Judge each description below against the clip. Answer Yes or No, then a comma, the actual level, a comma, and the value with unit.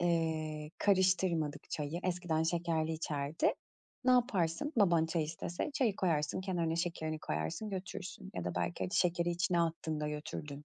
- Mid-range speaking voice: Yes, medium, 165 Hz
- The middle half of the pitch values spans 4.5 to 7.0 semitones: No, average, 2.8 semitones